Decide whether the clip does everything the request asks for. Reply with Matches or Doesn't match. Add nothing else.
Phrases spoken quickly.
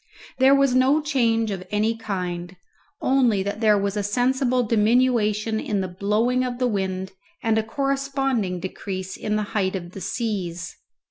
Doesn't match